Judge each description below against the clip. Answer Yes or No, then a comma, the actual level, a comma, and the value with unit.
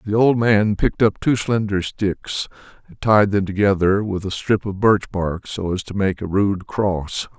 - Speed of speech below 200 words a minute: No, fast, 205 wpm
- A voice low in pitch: Yes, low, 100 Hz